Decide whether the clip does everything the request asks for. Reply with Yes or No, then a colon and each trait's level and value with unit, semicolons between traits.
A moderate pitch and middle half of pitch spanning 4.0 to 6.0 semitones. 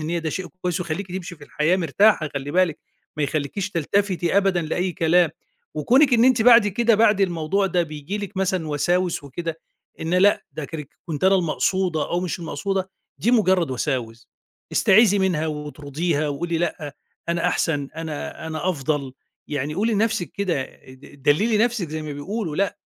Yes: medium, 175 Hz; average, 4.3 semitones